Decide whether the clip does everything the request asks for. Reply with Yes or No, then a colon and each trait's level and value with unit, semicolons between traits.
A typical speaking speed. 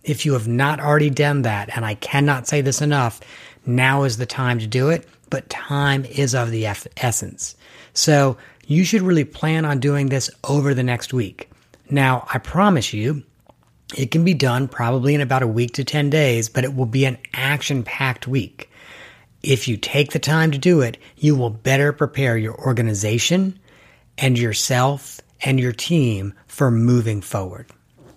Yes: average, 180 wpm